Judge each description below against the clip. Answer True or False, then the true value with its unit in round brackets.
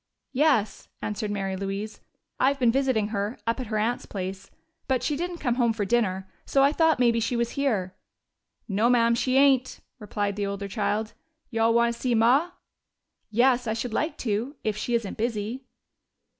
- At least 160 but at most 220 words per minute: True (185 wpm)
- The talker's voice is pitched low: False (230 Hz)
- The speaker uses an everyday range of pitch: True (3.6 semitones)